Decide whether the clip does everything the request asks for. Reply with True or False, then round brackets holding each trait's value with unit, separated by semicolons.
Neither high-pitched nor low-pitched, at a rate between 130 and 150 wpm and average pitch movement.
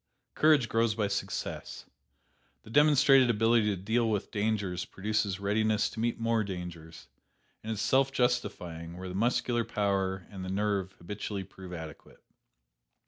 False (105 Hz; 140 wpm; 3.5 semitones)